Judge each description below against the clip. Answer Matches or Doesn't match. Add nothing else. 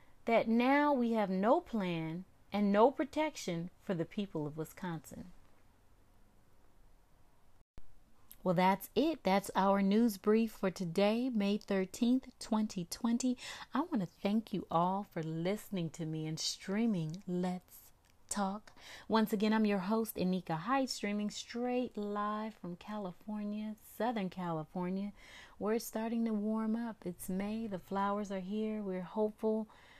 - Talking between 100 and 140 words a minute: Matches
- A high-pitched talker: Matches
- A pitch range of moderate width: Matches